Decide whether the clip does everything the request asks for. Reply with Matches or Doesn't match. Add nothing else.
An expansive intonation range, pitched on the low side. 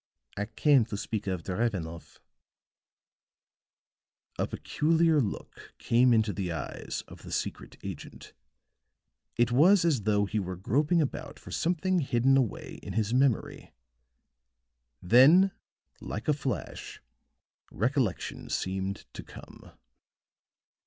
Matches